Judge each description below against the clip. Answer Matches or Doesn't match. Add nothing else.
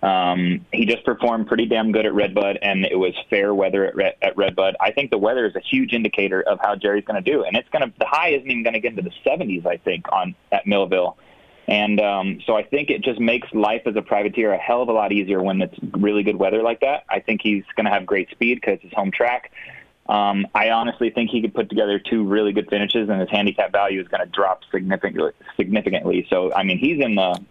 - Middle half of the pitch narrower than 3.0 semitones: Matches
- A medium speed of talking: Doesn't match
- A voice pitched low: Matches